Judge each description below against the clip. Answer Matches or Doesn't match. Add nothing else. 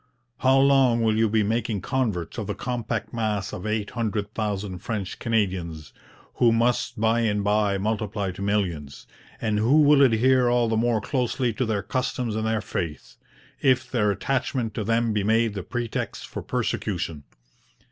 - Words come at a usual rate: Matches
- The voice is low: Matches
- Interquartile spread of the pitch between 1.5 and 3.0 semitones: Matches